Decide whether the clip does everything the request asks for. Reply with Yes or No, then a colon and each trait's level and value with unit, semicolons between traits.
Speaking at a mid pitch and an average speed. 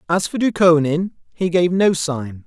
Yes: medium, 170 Hz; average, 170 wpm